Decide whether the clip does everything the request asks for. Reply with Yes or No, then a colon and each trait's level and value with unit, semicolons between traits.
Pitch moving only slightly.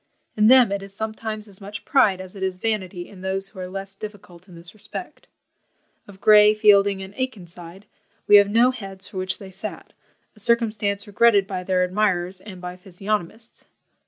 Yes: narrow, 2.2 semitones